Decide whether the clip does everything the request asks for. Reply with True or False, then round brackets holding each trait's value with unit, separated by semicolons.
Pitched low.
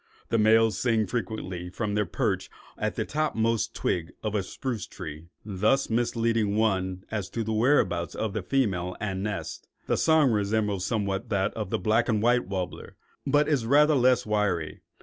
True (110 Hz)